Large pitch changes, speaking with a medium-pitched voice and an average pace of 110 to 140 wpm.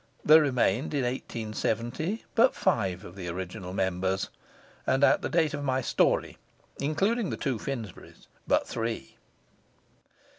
No: wide, 7.4 semitones; low, 120 Hz; slow, 135 wpm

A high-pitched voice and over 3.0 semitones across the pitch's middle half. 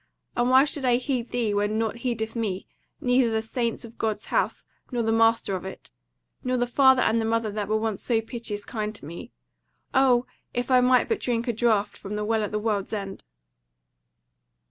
No: high, 225 Hz; narrow, 2.5 semitones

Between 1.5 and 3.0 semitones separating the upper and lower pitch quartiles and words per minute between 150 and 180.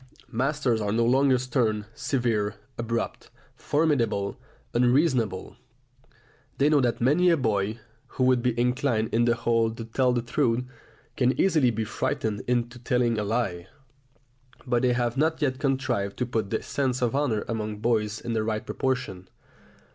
Yes: average, 2.7 semitones; average, 155 wpm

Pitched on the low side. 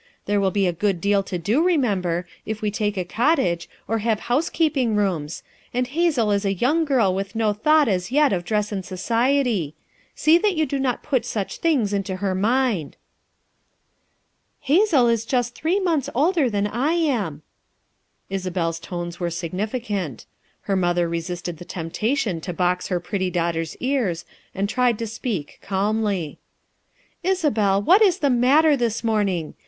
No: high, 210 Hz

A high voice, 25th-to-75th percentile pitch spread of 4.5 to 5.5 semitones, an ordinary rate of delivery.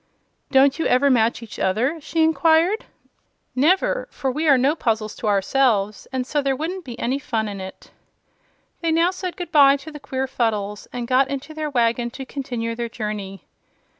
Yes: very high, 265 Hz; average, 5.1 semitones; average, 180 wpm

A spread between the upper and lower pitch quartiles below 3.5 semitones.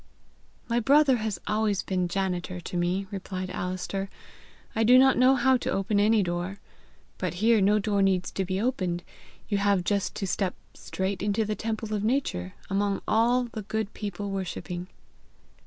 Yes: average, 2.9 semitones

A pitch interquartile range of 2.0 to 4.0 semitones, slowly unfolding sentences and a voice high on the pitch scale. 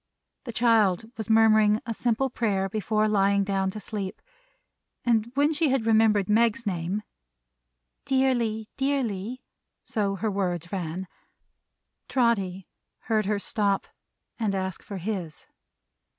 Yes: average, 2.9 semitones; slow, 120 wpm; high, 215 Hz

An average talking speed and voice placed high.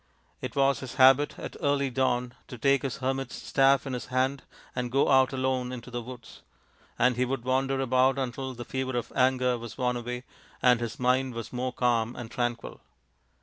No: average, 190 wpm; low, 130 Hz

